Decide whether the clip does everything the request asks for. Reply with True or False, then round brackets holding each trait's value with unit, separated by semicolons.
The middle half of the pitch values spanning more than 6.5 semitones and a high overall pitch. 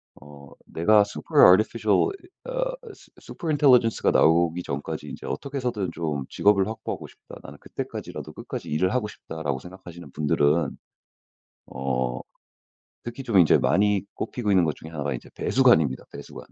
False (7.7 semitones; 90 Hz)